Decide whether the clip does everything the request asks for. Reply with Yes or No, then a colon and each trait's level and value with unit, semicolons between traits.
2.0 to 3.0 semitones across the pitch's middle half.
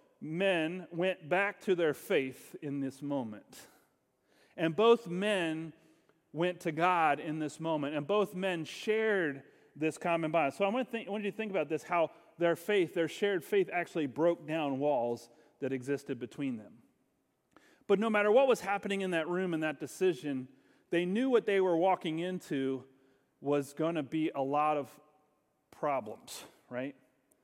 No: average, 4.3 semitones